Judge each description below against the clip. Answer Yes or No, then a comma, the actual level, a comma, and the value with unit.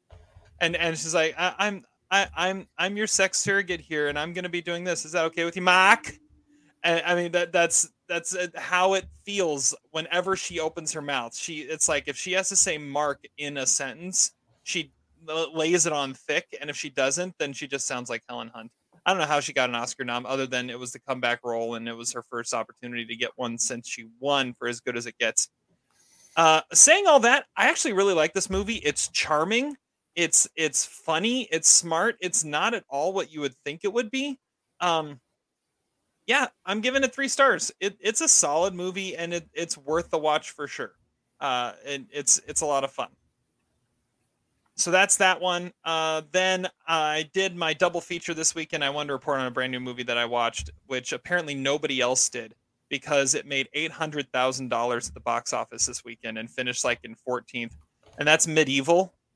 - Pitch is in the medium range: Yes, medium, 155 Hz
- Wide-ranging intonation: Yes, wide, 5.8 semitones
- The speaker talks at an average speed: No, fast, 210 wpm